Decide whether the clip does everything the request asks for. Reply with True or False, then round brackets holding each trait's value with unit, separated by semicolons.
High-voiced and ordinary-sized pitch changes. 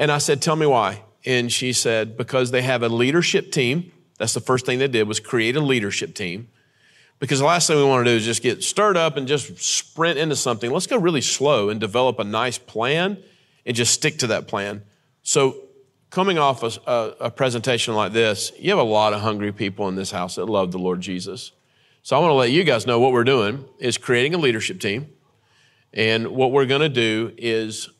False (125 Hz; 4.5 semitones)